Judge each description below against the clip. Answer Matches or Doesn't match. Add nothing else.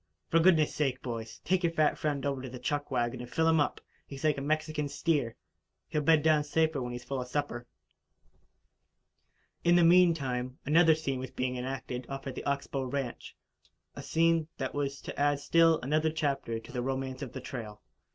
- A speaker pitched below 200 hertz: Matches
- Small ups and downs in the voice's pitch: Doesn't match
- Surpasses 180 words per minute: Matches